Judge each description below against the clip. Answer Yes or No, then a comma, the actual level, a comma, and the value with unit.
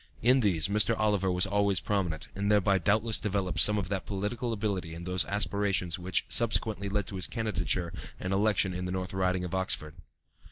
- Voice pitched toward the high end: No, low, 100 Hz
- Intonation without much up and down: Yes, narrow, 2.2 semitones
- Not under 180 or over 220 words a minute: Yes, average, 190 wpm